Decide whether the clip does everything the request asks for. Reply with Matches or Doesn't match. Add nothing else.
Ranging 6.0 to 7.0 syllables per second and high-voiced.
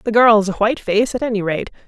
Matches